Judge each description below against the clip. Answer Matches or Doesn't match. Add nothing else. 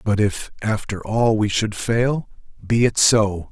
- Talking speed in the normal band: Matches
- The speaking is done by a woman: Doesn't match